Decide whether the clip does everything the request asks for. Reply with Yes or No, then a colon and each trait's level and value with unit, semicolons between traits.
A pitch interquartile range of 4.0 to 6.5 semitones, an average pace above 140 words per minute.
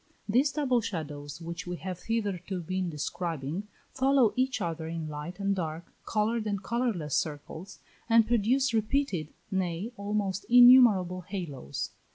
No: wide, 5.4 semitones; slow, 135 wpm